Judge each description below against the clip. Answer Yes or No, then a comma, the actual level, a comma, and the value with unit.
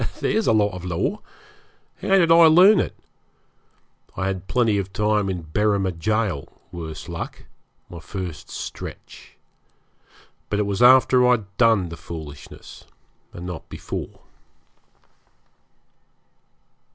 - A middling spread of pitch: Yes, average, 4.7 semitones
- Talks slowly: Yes, slow, 120 wpm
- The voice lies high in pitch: No, low, 100 Hz